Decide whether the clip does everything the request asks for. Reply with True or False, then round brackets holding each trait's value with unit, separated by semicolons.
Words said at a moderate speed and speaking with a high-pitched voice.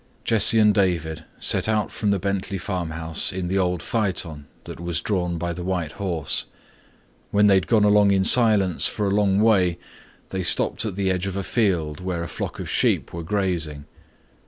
False (190 wpm; 95 Hz)